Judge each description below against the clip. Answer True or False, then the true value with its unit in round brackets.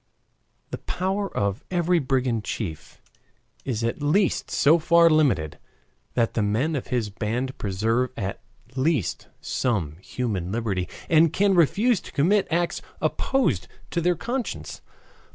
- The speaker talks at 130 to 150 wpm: True (135 wpm)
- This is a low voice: True (130 Hz)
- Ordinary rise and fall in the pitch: False (7.8 semitones)